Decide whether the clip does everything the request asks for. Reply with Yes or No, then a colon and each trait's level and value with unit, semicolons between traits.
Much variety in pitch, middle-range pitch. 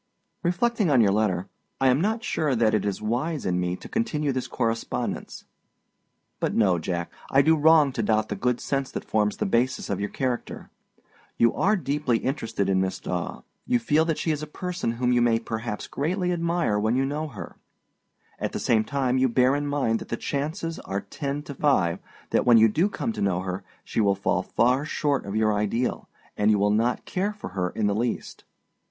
No: wide, 6.2 semitones; low, 125 Hz